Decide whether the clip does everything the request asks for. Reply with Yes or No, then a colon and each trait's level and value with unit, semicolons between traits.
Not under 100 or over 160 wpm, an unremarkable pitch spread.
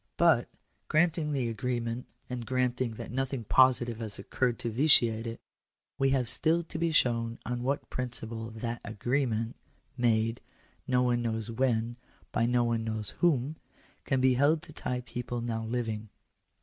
No: average, 155 wpm; narrow, 2.3 semitones